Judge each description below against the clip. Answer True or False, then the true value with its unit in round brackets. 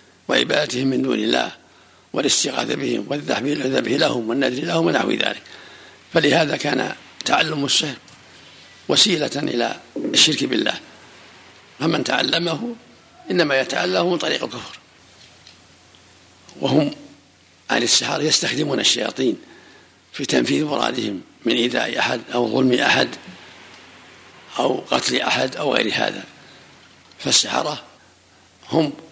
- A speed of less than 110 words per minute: True (100 wpm)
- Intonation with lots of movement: True (8.4 semitones)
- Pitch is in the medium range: False (130 Hz)